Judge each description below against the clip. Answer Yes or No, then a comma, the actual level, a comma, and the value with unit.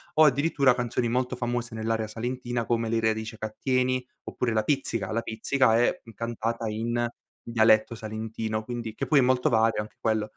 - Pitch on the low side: Yes, low, 115 Hz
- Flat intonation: Yes, narrow, 2.0 semitones